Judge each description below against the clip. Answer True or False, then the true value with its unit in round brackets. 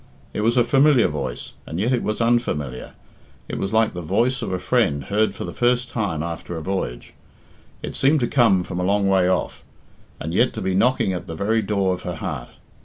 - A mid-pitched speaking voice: False (100 Hz)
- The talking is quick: True (220 wpm)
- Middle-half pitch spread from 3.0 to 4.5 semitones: False (5.2 semitones)